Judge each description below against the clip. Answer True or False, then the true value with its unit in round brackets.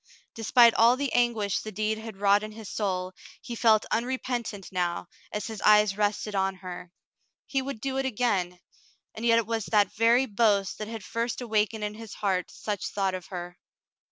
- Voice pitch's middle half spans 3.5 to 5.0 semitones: False (2.8 semitones)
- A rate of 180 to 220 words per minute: True (185 wpm)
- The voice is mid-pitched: False (215 Hz)